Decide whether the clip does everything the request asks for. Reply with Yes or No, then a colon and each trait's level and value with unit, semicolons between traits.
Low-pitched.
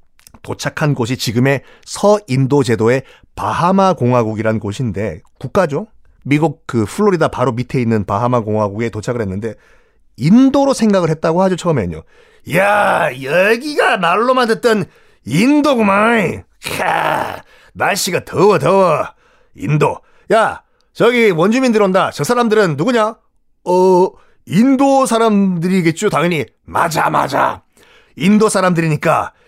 No: medium, 180 Hz